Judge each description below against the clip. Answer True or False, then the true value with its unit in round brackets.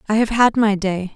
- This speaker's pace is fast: True (260 wpm)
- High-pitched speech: True (210 Hz)